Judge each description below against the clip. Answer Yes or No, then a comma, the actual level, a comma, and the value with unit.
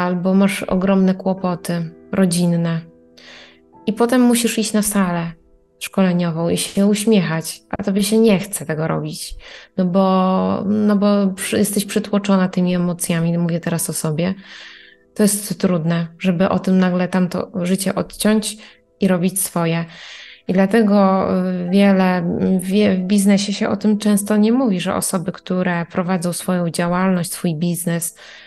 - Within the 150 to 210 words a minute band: No, average, 140 wpm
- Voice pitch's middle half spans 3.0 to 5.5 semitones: No, narrow, 2.6 semitones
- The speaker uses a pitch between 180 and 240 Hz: Yes, high, 190 Hz